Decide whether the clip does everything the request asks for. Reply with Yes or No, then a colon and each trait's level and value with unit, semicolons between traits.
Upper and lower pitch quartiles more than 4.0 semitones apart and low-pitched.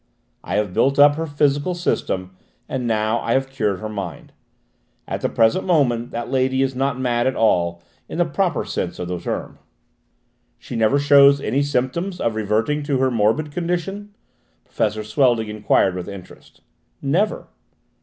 Yes: average, 5.0 semitones; low, 130 Hz